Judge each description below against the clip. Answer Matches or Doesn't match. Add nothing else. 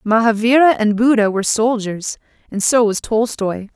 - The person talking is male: Doesn't match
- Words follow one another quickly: Doesn't match